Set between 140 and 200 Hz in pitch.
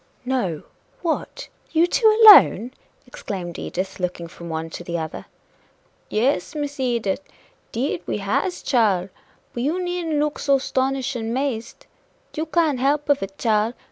No: very high, 250 Hz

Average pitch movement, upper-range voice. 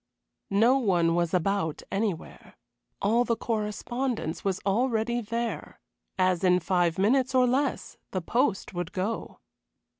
Yes: average, 4.6 semitones; high, 205 Hz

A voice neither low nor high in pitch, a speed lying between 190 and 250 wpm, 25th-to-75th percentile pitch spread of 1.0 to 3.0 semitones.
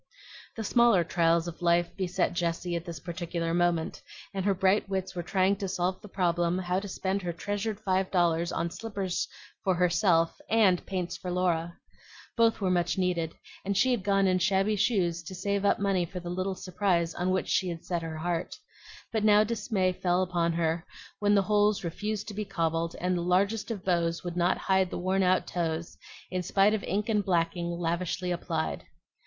Yes: medium, 180 Hz; average, 195 wpm; narrow, 2.4 semitones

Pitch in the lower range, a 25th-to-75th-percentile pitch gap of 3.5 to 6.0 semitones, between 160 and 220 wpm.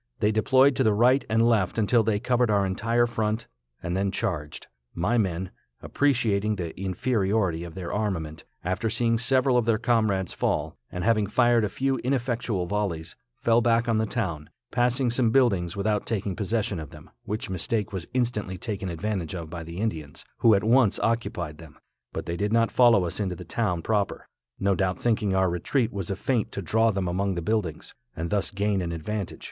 Yes: low, 105 Hz; average, 4.1 semitones; average, 195 wpm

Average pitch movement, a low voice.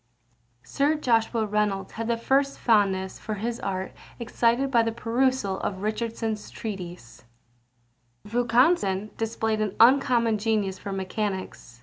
No: average, 3.0 semitones; high, 220 Hz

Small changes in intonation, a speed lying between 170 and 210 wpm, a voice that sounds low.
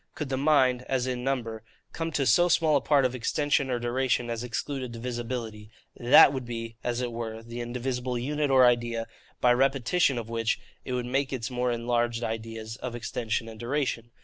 Yes: narrow, 2.2 semitones; average, 190 wpm; low, 125 Hz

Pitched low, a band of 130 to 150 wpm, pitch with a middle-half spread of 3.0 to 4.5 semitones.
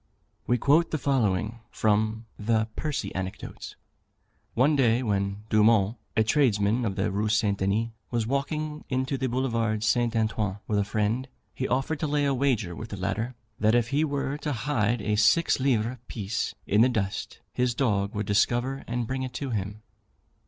No: low, 115 Hz; average, 175 wpm; average, 3.8 semitones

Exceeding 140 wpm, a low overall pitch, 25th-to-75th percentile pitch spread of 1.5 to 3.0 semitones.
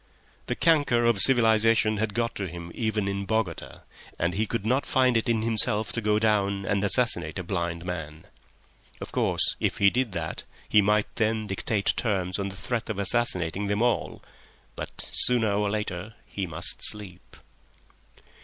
Yes: average, 165 wpm; low, 105 Hz; average, 2.7 semitones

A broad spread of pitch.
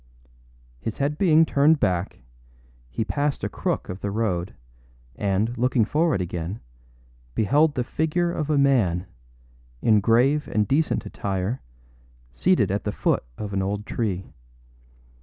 Yes: wide, 6.9 semitones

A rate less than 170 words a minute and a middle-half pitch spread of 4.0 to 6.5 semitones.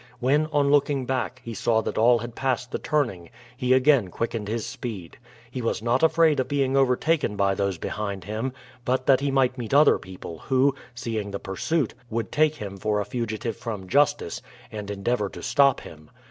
No: average, 190 wpm; average, 4.7 semitones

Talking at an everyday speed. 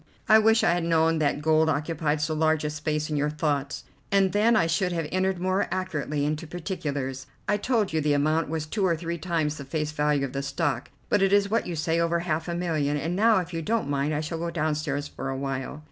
No: fast, 240 wpm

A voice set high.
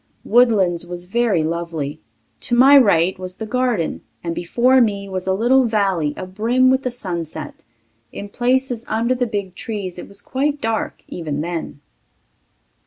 Yes: high, 200 Hz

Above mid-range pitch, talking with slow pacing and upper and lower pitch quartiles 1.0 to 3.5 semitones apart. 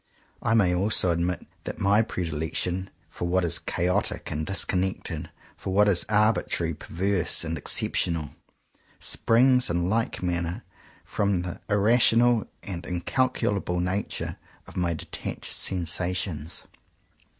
No: very low, 90 Hz; slow, 120 wpm; average, 3.1 semitones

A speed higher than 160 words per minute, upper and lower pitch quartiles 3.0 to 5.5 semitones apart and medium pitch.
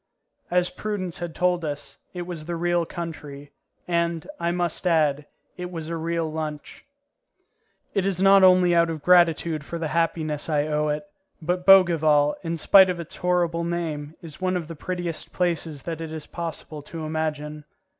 No: average, 175 wpm; narrow, 2.4 semitones; medium, 165 Hz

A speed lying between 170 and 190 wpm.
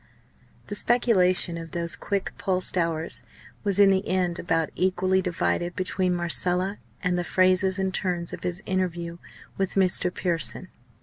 No: average, 145 wpm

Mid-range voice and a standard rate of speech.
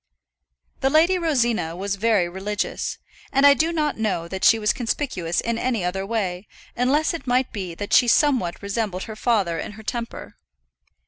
No: high, 220 Hz; average, 175 wpm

